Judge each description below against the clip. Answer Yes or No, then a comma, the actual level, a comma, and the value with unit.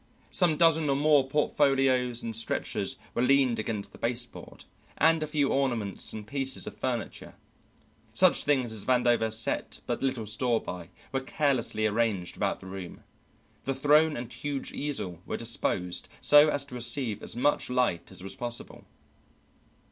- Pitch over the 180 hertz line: No, low, 125 Hz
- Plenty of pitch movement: No, average, 4.0 semitones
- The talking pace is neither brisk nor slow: Yes, average, 155 wpm